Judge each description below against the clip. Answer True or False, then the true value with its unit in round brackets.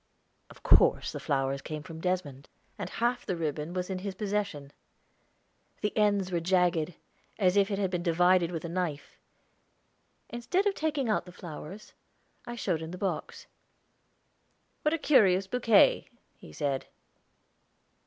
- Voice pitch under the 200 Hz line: True (185 Hz)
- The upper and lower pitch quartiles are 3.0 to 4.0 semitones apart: False (4.4 semitones)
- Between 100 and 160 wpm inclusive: True (150 wpm)